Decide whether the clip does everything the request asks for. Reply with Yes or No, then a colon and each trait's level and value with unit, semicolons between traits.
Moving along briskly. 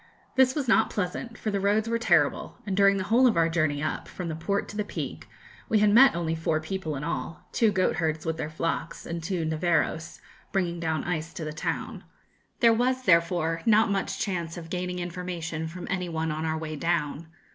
Yes: fast, 210 wpm